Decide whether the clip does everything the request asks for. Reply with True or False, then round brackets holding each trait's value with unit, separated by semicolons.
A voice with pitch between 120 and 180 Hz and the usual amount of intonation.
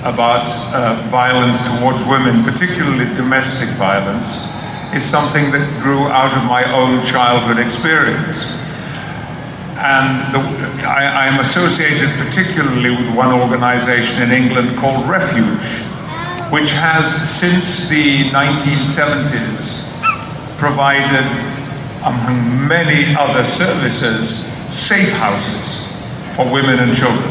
True (135 Hz; 3.1 semitones)